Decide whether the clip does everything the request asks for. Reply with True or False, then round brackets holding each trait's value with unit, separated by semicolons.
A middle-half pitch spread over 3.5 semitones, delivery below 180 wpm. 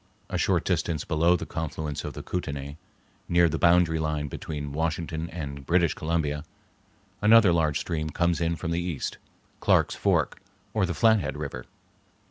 False (2.4 semitones; 155 wpm)